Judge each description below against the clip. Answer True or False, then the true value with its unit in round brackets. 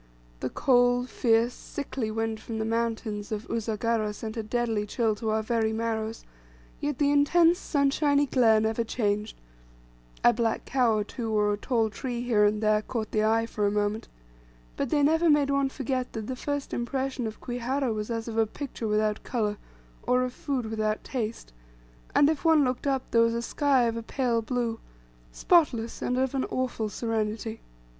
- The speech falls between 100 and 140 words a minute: False (185 wpm)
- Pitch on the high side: True (230 Hz)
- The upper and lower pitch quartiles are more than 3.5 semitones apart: False (3.0 semitones)